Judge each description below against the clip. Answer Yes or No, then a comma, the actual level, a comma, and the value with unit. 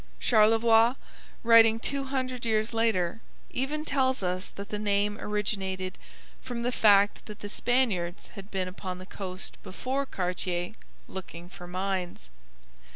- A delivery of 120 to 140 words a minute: Yes, slow, 135 wpm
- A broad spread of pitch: No, average, 4.1 semitones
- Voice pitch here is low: No, high, 210 Hz